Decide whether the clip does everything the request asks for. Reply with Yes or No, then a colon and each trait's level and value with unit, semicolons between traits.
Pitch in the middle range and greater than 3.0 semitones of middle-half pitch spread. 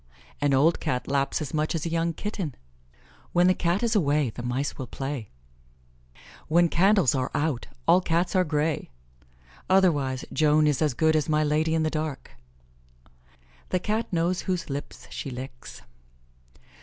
Yes: medium, 155 Hz; average, 3.6 semitones